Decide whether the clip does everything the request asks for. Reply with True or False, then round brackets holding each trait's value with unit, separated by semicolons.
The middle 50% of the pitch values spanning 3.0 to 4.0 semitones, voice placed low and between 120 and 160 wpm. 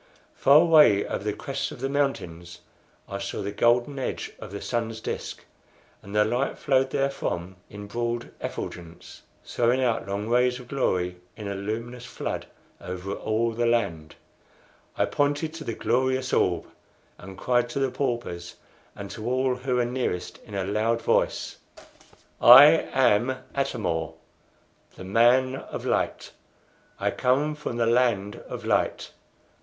False (4.5 semitones; 120 Hz; 150 wpm)